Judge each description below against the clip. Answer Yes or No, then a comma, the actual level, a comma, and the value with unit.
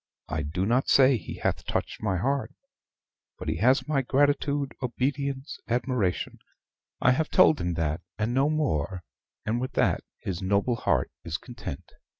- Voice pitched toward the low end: Yes, low, 125 Hz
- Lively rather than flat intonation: Yes, wide, 6.7 semitones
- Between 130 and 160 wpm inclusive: Yes, average, 155 wpm